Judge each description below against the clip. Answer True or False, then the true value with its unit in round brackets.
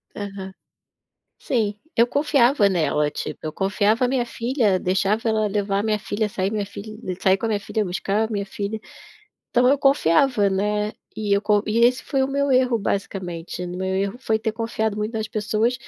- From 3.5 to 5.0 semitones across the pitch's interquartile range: False (2.9 semitones)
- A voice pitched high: True (210 Hz)